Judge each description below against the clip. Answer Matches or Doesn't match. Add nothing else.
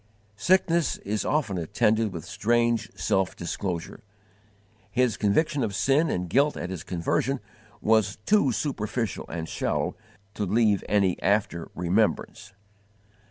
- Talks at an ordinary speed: Doesn't match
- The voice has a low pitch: Matches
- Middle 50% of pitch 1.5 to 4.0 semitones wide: Doesn't match